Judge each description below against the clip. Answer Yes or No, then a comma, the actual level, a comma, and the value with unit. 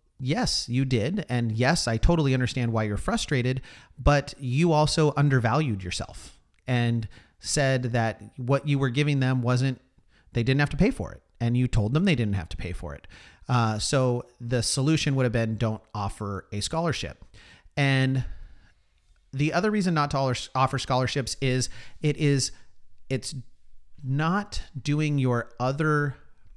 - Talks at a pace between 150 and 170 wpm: Yes, average, 160 wpm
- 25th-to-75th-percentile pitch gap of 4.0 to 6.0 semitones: Yes, average, 4.5 semitones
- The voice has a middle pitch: No, low, 125 Hz